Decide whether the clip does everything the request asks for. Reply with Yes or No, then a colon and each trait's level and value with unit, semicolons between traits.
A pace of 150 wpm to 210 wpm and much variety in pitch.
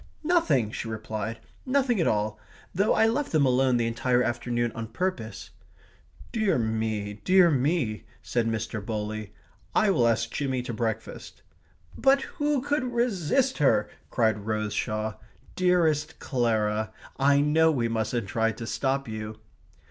No: average, 140 wpm; wide, 7.5 semitones